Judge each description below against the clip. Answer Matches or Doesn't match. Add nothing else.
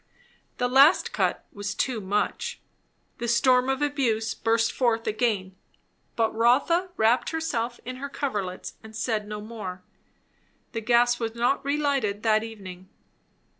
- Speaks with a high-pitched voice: Matches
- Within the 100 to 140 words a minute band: Matches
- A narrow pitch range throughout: Doesn't match